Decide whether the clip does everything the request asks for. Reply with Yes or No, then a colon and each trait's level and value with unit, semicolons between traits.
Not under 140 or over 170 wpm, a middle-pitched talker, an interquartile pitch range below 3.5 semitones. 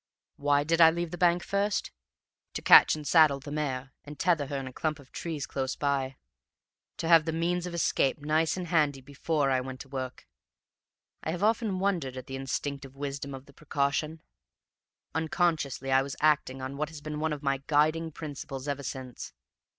No: average, 190 wpm; medium, 145 Hz; average, 3.0 semitones